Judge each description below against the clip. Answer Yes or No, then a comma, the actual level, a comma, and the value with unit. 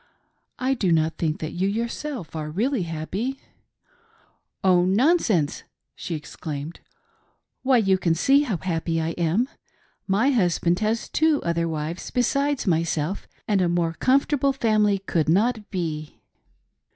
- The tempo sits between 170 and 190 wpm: No, average, 145 wpm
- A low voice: No, medium, 185 Hz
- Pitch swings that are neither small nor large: No, wide, 6.7 semitones